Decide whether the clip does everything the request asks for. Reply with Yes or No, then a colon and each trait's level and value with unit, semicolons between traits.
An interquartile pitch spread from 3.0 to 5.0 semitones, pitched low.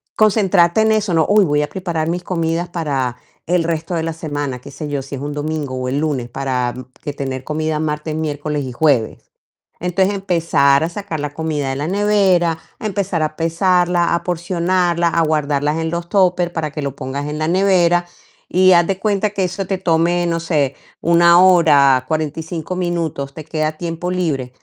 No: average, 3.3 semitones; medium, 165 Hz